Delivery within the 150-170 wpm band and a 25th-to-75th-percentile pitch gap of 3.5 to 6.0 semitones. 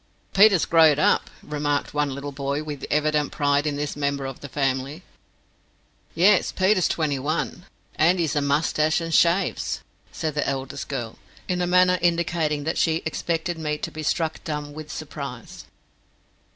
No: average, 160 wpm; average, 2.7 semitones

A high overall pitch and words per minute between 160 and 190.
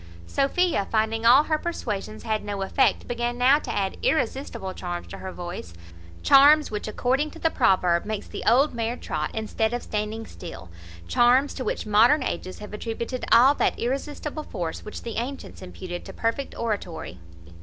Yes: high, 225 Hz; average, 170 wpm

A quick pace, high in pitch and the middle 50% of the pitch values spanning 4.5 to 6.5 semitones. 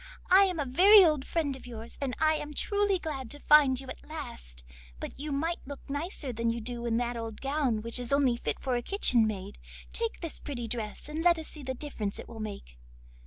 Yes: fast, 230 wpm; very high, 270 Hz; average, 4.9 semitones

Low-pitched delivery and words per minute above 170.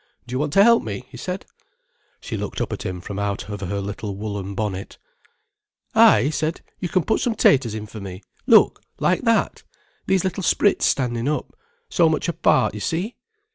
Yes: low, 125 Hz; average, 180 wpm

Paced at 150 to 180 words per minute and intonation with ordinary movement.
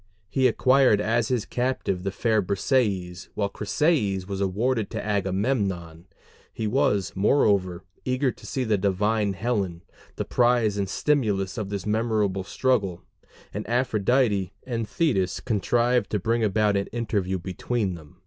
No: average, 140 wpm; average, 3.8 semitones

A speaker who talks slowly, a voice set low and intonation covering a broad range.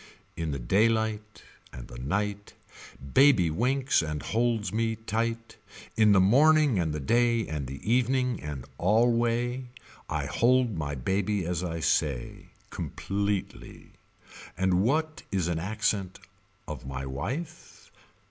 Yes: slow, 130 wpm; low, 105 Hz; wide, 6.4 semitones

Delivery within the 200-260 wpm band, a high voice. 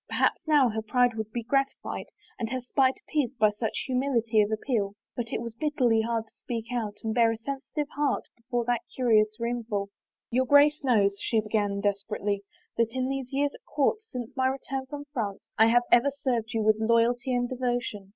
Yes: fast, 205 wpm; high, 235 Hz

